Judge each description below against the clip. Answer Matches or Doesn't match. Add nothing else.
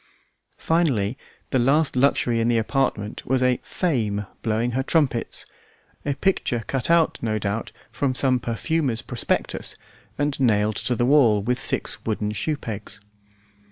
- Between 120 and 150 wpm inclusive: Matches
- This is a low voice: Matches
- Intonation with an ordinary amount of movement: Matches